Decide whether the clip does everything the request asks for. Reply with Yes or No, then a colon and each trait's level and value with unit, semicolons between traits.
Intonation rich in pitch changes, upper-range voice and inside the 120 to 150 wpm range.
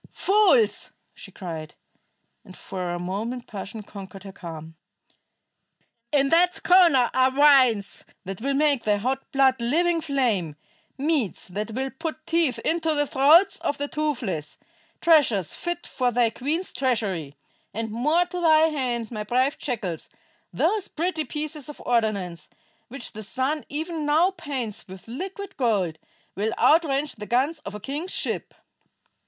Yes: wide, 6.7 semitones; very high, 260 Hz; average, 145 wpm